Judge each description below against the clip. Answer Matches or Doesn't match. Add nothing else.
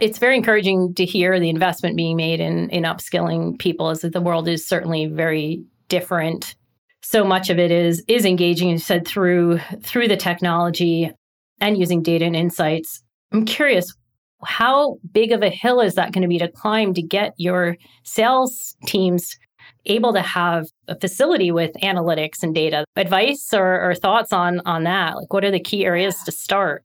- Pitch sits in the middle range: Matches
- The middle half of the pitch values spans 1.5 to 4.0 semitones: Matches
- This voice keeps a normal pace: Matches